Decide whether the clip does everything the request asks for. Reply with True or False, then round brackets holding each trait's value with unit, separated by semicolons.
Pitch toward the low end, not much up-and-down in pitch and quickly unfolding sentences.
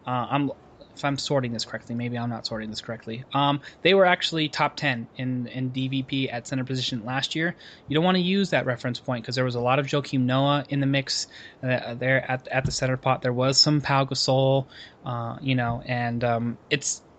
True (130 Hz; 2.3 semitones; 225 wpm)